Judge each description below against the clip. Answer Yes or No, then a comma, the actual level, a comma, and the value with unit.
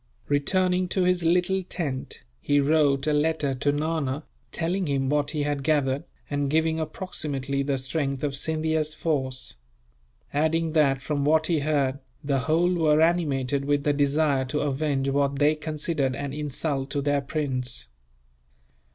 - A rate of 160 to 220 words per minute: No, average, 150 wpm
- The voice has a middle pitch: Yes, medium, 145 Hz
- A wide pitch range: No, narrow, 2.4 semitones